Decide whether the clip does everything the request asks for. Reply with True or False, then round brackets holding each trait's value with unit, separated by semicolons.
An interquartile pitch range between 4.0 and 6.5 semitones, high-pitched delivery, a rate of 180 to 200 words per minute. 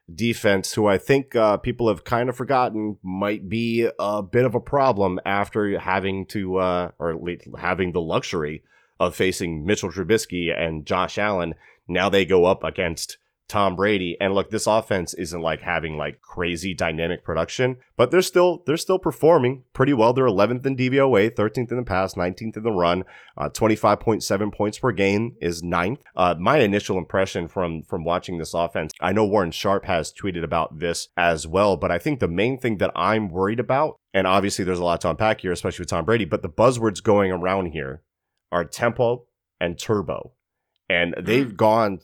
False (4.5 semitones; 100 Hz; 190 wpm)